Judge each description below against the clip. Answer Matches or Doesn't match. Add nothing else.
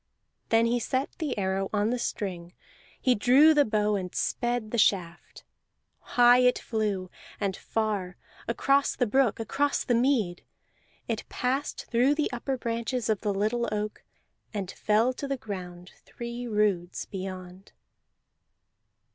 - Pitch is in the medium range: Doesn't match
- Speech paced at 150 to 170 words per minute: Doesn't match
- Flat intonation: Doesn't match